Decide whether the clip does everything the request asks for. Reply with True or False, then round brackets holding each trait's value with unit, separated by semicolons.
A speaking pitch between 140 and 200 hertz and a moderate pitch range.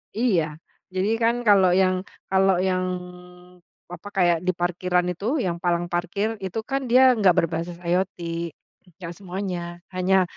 False (185 Hz; 2.0 semitones)